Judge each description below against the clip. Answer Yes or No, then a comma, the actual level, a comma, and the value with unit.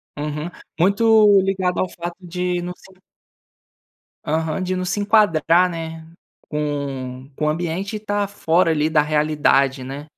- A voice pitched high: No, medium, 165 Hz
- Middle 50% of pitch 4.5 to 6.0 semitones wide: No, average, 3.7 semitones